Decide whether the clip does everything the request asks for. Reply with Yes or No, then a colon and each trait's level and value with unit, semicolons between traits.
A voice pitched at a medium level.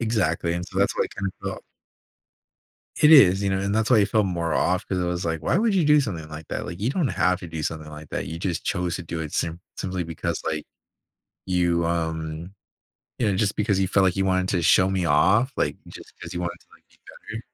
No: very low, 90 Hz